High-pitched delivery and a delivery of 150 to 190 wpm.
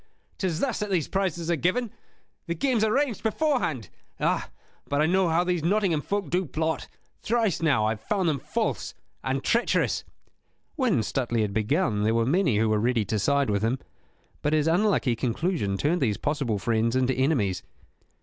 No: medium, 155 Hz; average, 180 wpm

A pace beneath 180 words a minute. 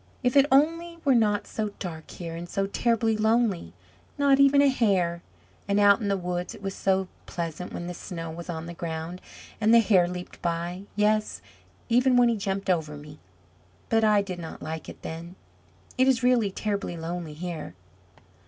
No: average, 185 wpm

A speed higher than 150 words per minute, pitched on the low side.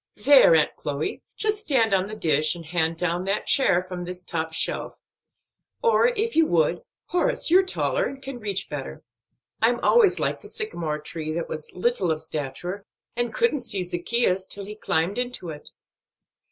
No: average, 175 wpm; high, 190 Hz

